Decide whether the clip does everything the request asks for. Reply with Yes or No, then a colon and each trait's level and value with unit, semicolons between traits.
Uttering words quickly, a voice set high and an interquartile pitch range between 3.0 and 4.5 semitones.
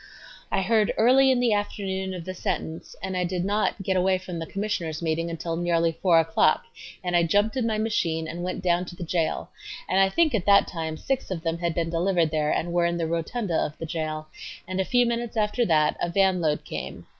No: fast, 230 wpm; medium, 180 Hz; average, 3.6 semitones